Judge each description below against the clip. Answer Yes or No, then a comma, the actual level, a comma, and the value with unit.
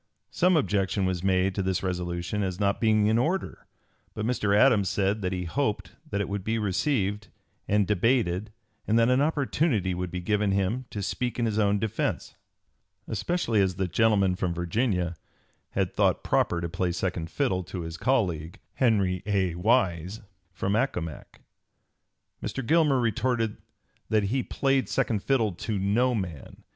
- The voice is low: Yes, low, 100 Hz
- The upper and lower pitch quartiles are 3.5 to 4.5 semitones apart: Yes, average, 4.0 semitones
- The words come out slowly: No, average, 155 wpm